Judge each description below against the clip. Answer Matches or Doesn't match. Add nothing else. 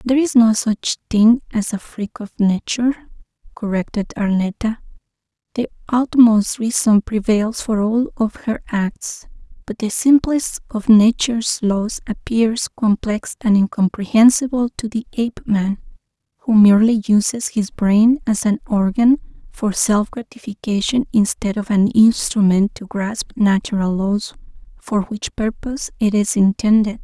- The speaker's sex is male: Doesn't match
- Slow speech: Matches